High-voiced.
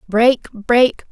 Yes: high, 230 Hz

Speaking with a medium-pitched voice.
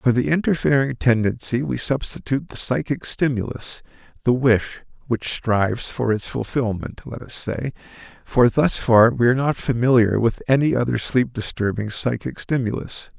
No: low, 120 Hz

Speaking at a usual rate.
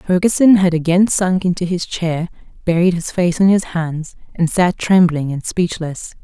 Yes: average, 175 wpm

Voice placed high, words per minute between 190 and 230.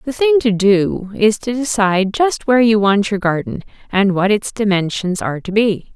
Yes: high, 210 Hz; average, 200 wpm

